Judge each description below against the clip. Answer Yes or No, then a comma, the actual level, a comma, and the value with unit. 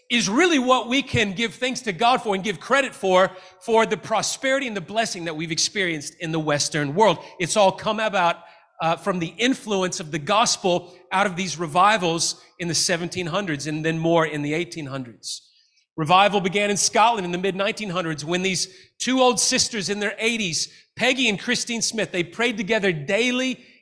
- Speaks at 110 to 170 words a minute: No, average, 190 wpm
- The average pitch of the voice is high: Yes, high, 195 Hz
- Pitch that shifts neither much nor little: Yes, average, 4.8 semitones